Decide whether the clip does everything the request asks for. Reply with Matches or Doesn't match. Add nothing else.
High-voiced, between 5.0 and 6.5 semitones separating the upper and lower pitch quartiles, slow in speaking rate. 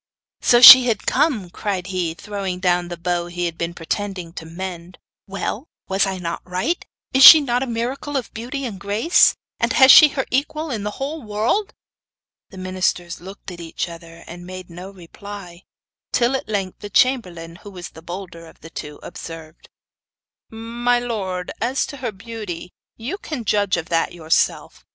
Doesn't match